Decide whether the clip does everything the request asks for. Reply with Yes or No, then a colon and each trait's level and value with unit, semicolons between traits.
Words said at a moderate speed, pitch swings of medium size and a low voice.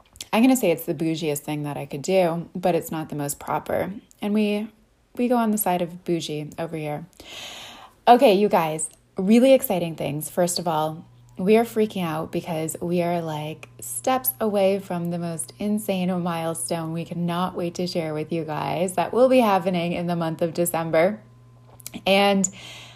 No: average, 185 wpm; average, 3.5 semitones; medium, 175 Hz